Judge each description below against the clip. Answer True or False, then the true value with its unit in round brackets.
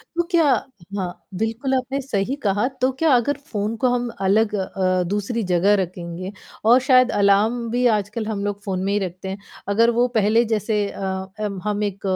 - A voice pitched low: False (210 Hz)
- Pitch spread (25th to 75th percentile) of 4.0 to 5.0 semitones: False (3.5 semitones)